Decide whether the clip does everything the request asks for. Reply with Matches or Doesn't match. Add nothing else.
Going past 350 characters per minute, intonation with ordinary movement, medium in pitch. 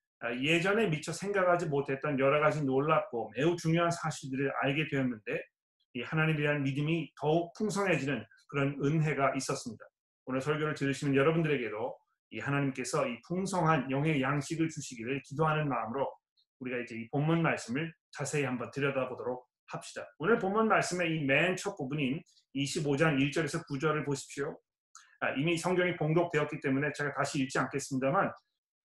Matches